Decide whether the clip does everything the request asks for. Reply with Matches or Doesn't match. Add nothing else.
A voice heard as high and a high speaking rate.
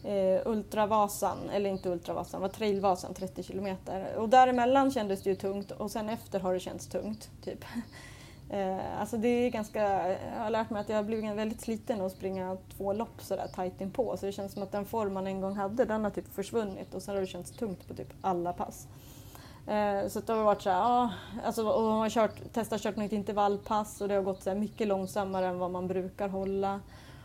Matches